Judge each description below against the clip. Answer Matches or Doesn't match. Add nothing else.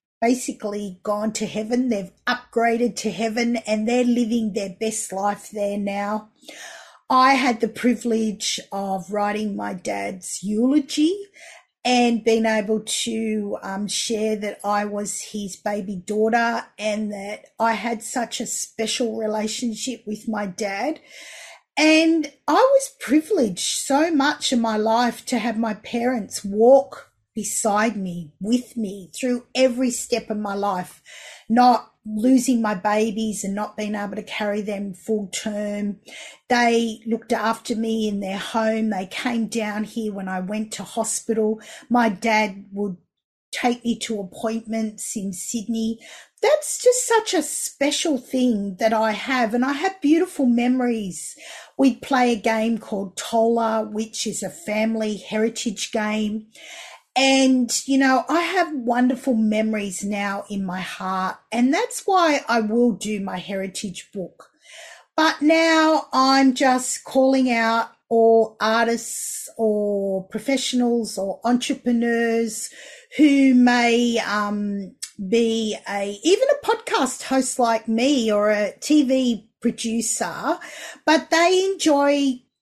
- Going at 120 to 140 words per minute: Matches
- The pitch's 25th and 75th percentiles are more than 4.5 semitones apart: Doesn't match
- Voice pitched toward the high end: Matches